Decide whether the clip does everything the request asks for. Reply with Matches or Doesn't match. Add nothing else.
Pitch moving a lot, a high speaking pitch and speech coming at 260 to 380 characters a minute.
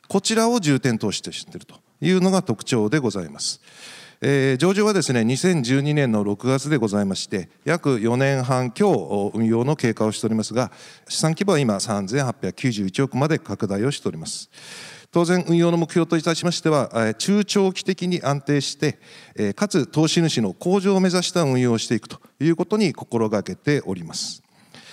Doesn't match